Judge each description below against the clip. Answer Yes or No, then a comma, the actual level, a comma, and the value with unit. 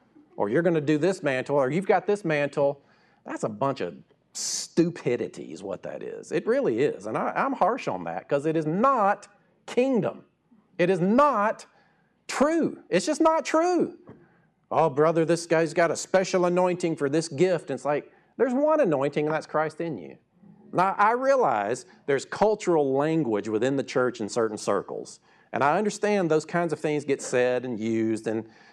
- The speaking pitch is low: No, medium, 170 Hz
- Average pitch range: No, wide, 6.4 semitones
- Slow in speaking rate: No, average, 185 wpm